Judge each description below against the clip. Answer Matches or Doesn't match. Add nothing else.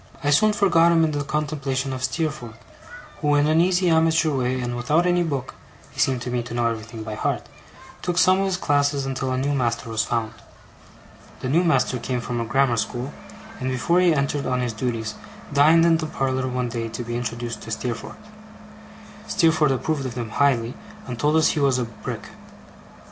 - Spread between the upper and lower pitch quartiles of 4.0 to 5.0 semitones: Matches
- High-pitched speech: Doesn't match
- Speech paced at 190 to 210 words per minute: Matches